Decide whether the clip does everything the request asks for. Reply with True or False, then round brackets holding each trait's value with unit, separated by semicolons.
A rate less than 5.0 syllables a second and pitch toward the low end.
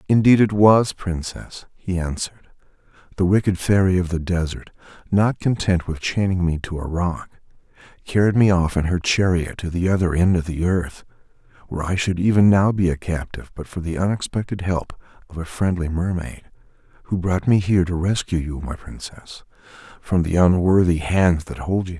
False (5.1 syllables/s; 90 Hz)